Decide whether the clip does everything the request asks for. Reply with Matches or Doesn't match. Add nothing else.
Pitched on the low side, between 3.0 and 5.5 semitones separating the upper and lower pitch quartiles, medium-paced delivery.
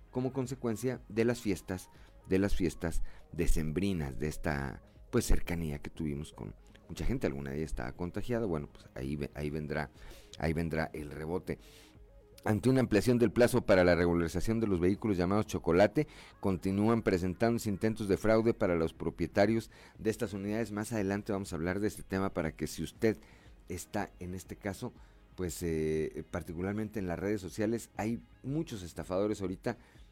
Matches